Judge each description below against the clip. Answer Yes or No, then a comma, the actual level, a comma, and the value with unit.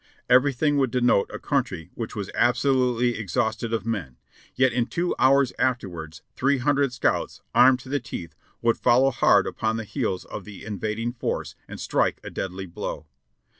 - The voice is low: Yes, low, 120 Hz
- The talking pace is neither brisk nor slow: Yes, average, 175 wpm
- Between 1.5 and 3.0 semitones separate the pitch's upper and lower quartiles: No, average, 3.8 semitones